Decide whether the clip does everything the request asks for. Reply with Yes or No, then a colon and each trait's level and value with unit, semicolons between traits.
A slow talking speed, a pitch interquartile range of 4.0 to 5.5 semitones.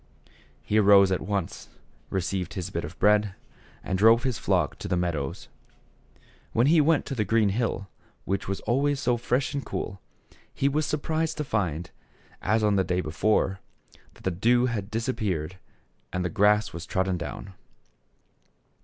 No: average, 165 wpm; average, 4.3 semitones